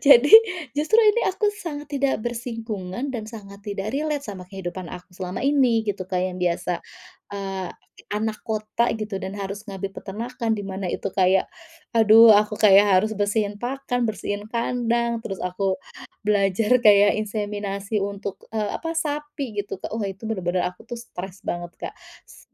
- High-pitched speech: Yes, high, 210 Hz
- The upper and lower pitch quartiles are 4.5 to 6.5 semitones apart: No, average, 3.4 semitones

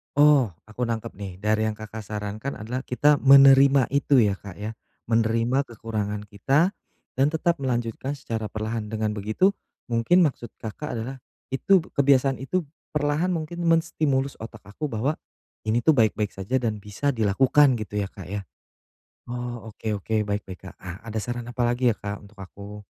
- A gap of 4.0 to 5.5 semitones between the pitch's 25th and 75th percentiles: Yes, average, 4.6 semitones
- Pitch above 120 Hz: No, low, 115 Hz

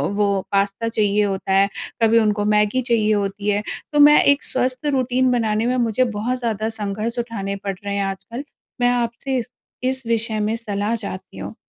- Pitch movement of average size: Yes, average, 3.2 semitones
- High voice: Yes, high, 220 Hz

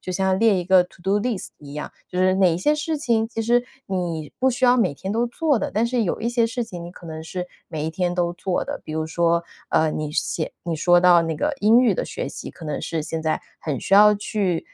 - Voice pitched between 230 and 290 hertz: No, medium, 185 Hz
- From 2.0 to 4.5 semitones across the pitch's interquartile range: No, wide, 5.4 semitones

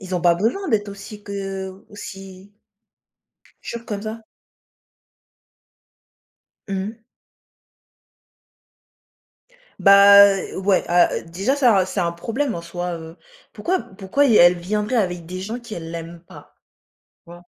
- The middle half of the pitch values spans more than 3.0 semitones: Yes, average, 3.5 semitones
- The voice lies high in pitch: Yes, high, 195 Hz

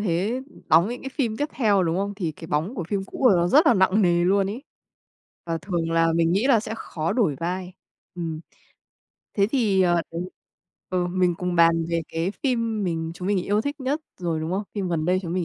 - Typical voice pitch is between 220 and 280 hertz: No, medium, 185 Hz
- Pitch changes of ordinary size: Yes, average, 4.1 semitones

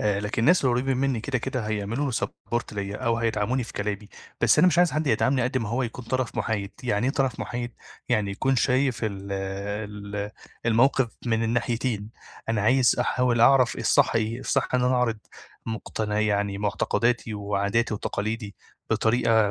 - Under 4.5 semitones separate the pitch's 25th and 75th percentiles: Yes, average, 3.4 semitones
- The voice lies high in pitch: No, low, 115 Hz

